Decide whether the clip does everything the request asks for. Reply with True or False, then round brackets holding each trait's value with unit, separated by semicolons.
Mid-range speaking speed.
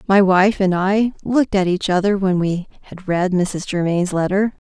True (195 wpm)